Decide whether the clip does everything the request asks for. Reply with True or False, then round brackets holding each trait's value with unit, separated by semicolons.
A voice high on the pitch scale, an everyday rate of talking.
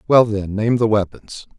False (110 Hz; 190 wpm)